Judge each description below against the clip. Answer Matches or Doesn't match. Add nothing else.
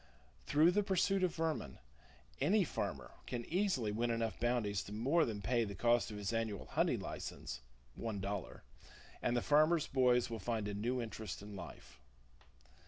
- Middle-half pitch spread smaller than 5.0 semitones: Doesn't match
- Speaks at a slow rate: Doesn't match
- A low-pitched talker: Matches